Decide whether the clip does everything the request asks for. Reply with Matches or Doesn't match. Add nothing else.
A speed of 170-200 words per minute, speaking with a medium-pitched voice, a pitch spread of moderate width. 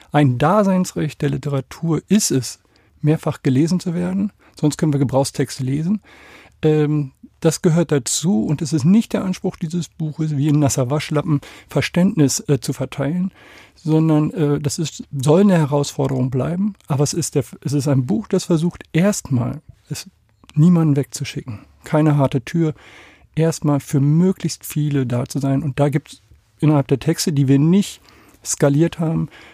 Doesn't match